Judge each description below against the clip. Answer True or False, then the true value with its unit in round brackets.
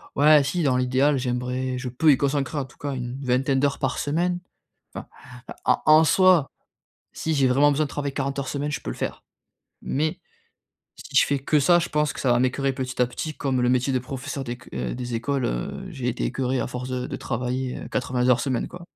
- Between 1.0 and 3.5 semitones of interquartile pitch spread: True (2.5 semitones)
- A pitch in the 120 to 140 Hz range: True (135 Hz)